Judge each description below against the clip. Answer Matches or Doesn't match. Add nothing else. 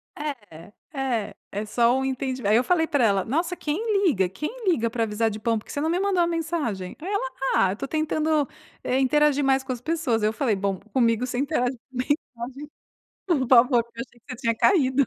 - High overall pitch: Matches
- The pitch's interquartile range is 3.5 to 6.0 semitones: Matches